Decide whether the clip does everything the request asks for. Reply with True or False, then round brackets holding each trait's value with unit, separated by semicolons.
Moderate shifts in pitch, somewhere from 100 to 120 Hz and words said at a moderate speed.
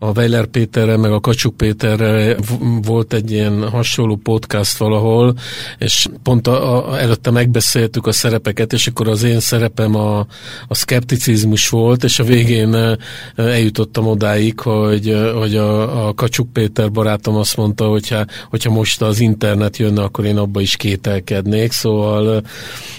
False (1.7 semitones; 110 Hz; 145 wpm)